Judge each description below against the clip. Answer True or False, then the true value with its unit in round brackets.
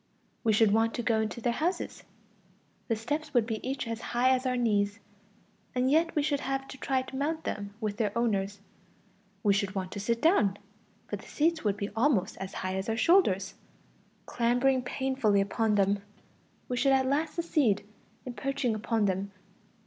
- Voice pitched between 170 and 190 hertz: False (235 Hz)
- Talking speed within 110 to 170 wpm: False (185 wpm)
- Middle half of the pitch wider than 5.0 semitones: False (4.7 semitones)